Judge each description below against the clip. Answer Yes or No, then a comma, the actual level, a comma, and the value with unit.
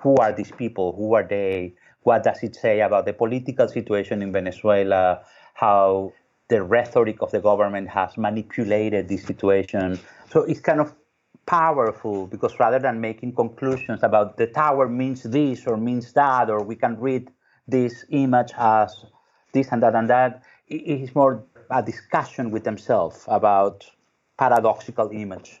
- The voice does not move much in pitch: No, average, 4.2 semitones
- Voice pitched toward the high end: No, low, 110 Hz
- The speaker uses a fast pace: No, average, 155 wpm